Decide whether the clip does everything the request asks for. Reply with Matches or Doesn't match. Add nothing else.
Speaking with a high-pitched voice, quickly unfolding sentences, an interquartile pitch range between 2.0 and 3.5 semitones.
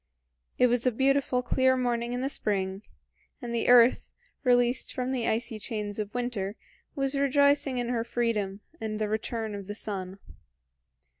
Doesn't match